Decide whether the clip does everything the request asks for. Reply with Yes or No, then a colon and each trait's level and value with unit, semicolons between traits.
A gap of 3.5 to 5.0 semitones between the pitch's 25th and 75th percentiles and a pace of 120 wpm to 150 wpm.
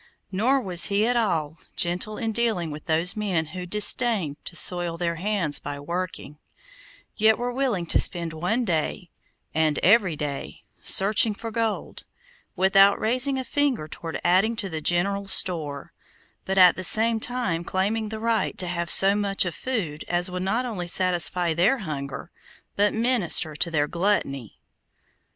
No: average, 4.6 semitones; average, 160 wpm